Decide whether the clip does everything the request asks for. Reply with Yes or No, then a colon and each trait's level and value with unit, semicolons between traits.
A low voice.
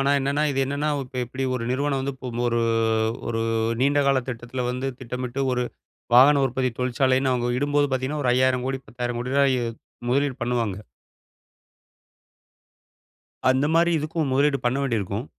Yes: low, 130 Hz